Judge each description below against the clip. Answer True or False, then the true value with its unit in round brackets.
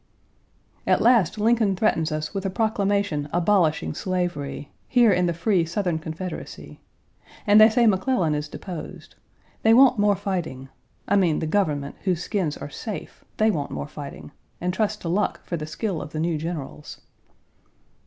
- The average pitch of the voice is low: False (180 Hz)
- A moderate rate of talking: True (165 wpm)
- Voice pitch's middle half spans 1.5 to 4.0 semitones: False (4.9 semitones)